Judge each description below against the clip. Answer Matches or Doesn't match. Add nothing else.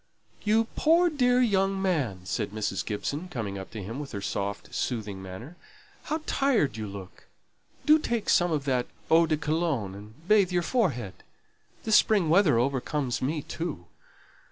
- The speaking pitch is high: Doesn't match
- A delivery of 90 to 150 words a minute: Doesn't match